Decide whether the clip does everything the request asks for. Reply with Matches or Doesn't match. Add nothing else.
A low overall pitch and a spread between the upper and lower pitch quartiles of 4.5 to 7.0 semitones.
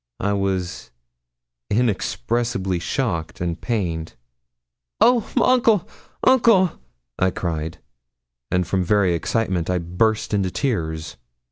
Matches